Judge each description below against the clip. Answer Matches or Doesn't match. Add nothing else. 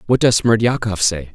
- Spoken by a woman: Doesn't match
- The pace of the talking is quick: Doesn't match